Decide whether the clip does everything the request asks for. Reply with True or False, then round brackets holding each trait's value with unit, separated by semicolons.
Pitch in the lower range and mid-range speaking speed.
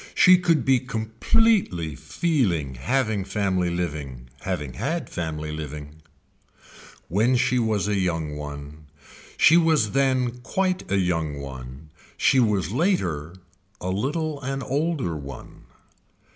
False (95 Hz; 120 wpm)